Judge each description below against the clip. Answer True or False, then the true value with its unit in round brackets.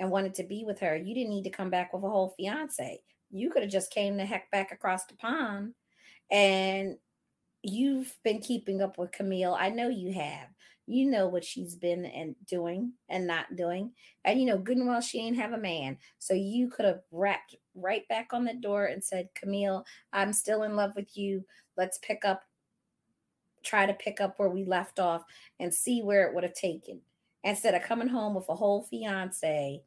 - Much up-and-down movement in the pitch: False (3.0 semitones)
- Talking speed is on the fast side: True (210 wpm)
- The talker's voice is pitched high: True (195 Hz)